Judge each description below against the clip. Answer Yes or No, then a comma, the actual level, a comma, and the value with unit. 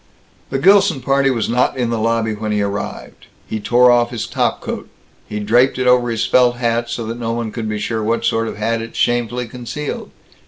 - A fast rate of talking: Yes, fast, 220 wpm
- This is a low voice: Yes, low, 120 Hz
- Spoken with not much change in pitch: Yes, narrow, 1.9 semitones